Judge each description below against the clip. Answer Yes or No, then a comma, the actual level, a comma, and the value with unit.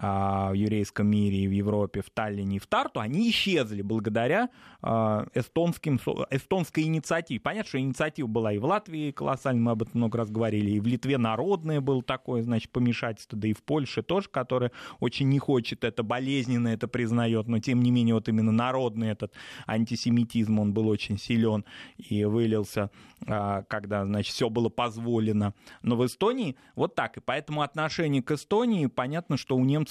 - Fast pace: Yes, fast, 175 wpm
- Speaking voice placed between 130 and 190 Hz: No, low, 120 Hz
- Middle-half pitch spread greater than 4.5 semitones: No, average, 4.0 semitones